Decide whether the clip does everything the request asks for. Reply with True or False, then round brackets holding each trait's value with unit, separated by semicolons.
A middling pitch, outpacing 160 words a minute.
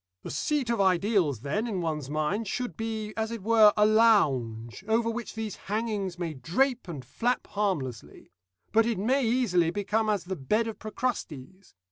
False (210 Hz; 170 wpm)